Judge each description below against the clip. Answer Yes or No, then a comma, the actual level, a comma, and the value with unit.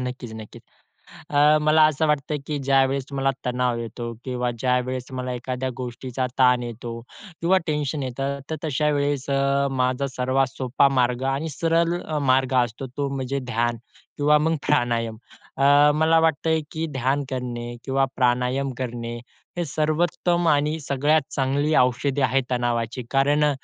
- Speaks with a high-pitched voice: No, low, 135 Hz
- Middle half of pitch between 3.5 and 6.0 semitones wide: No, average, 2.8 semitones